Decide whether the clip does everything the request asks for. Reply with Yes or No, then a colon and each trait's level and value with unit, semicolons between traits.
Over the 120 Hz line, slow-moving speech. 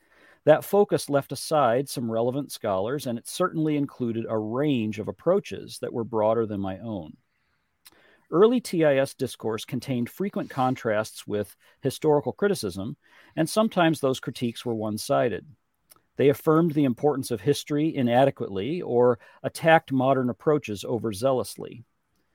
Yes: low, 135 Hz; slow, 130 wpm